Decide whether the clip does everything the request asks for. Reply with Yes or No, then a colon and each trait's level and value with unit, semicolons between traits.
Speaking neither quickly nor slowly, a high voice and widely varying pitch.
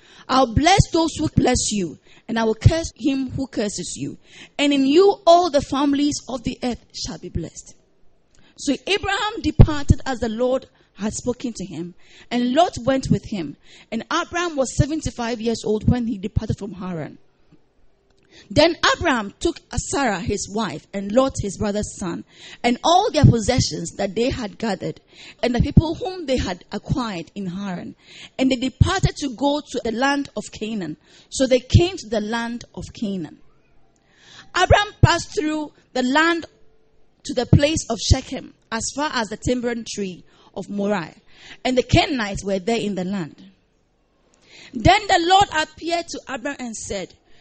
Yes: average, 165 wpm; very high, 250 Hz; wide, 5.8 semitones